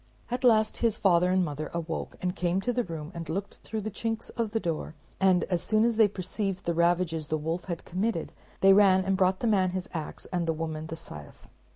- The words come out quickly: Yes, fast, 230 wpm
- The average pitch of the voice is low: No, medium, 185 Hz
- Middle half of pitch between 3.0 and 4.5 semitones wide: Yes, average, 3.9 semitones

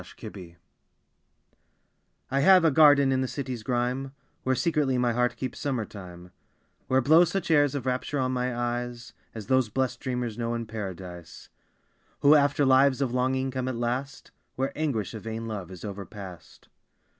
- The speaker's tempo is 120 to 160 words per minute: No, average, 170 wpm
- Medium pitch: No, low, 125 Hz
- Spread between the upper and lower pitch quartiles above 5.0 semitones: No, average, 3.4 semitones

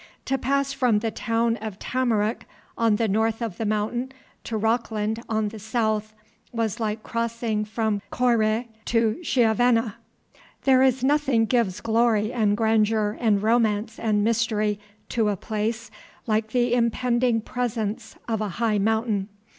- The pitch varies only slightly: Yes, narrow, 1.8 semitones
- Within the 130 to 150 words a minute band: Yes, average, 145 wpm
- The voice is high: Yes, high, 225 Hz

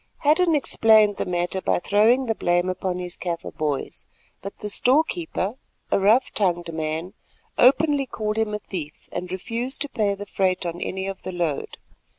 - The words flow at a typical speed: Yes, average, 170 wpm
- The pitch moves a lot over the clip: No, average, 4.8 semitones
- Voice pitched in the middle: No, high, 200 Hz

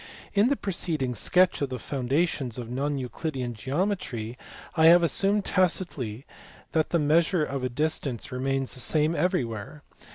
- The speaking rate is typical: Yes, average, 150 wpm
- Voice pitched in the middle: Yes, medium, 145 Hz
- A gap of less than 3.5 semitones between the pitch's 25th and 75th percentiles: No, average, 5.2 semitones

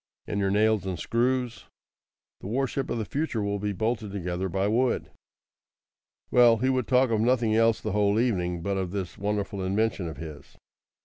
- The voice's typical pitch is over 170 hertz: No, low, 105 Hz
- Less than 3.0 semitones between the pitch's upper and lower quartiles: No, average, 3.4 semitones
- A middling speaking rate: Yes, average, 180 wpm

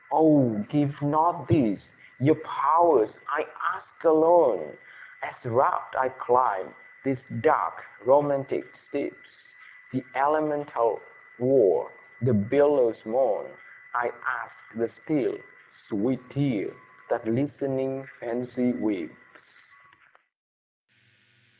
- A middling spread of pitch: Yes, average, 3.2 semitones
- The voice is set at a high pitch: No, low, 135 Hz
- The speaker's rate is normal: No, slow, 90 wpm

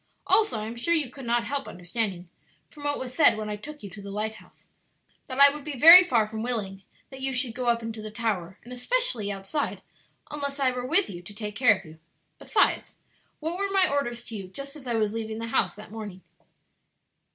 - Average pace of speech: No, fast, 225 wpm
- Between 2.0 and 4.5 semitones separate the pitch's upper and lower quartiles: No, average, 4.9 semitones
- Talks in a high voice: Yes, high, 235 Hz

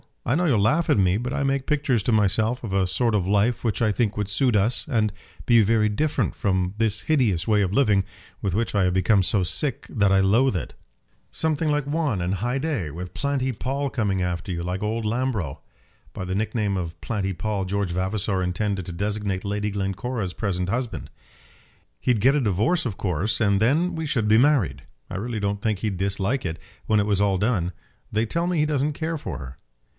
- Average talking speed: No, fast, 210 wpm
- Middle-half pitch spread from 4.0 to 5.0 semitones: Yes, average, 4.6 semitones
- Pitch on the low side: Yes, low, 105 Hz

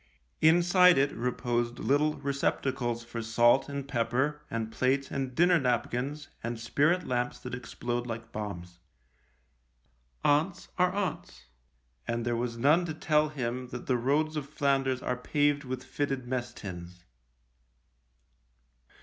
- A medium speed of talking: No, slow, 130 wpm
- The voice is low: Yes, low, 130 Hz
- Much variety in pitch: No, average, 3.6 semitones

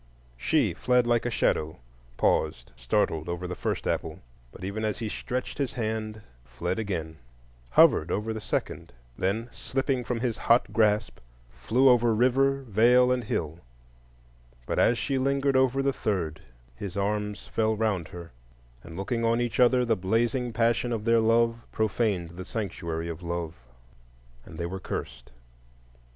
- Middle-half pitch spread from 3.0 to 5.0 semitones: No, wide, 5.4 semitones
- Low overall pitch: Yes, low, 110 Hz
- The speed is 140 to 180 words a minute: Yes, average, 155 wpm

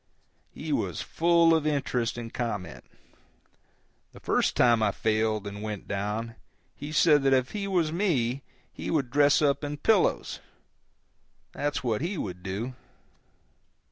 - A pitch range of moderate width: No, wide, 5.8 semitones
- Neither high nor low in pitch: No, low, 130 Hz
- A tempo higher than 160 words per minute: No, average, 140 wpm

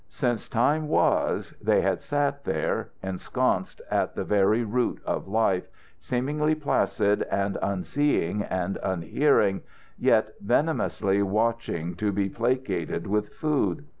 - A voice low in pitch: Yes, low, 105 Hz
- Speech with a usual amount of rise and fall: No, wide, 6.1 semitones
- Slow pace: Yes, slow, 120 wpm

